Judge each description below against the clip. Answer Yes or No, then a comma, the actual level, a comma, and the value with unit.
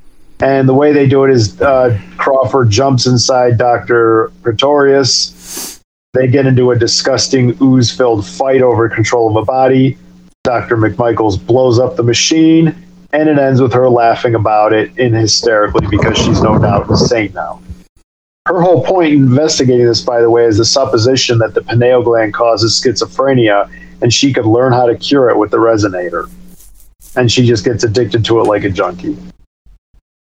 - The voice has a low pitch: Yes, low, 120 Hz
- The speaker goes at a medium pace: Yes, average, 170 wpm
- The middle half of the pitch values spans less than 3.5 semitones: Yes, average, 3.0 semitones